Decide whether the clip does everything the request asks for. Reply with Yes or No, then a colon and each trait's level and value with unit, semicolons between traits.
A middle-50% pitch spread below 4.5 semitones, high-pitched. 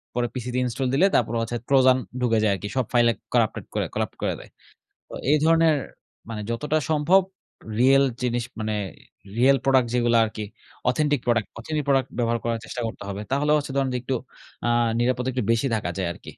No: average, 2.8 semitones; low, 125 Hz